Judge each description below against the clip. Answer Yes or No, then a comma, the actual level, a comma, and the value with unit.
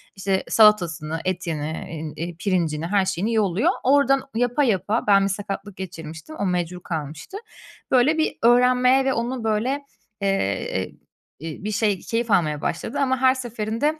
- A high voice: Yes, high, 205 Hz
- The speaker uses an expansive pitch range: Yes, wide, 5.9 semitones